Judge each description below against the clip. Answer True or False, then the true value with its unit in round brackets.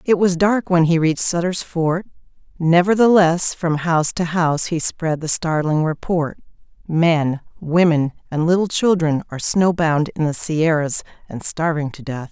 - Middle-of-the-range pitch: True (165 Hz)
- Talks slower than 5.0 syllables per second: True (4.6 syllables/s)